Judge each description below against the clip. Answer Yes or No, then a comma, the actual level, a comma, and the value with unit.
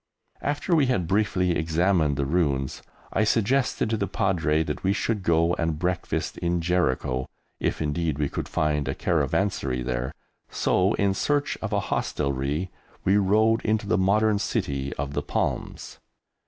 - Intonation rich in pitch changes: Yes, wide, 5.7 semitones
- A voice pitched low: Yes, very low, 90 Hz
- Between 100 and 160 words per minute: Yes, average, 155 wpm